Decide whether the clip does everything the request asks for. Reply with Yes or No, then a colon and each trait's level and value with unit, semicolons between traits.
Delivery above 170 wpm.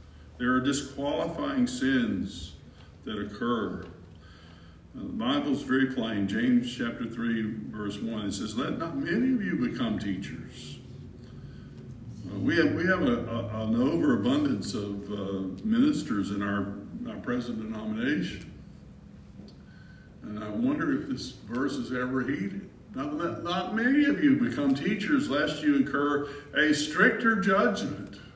No: slow, 135 wpm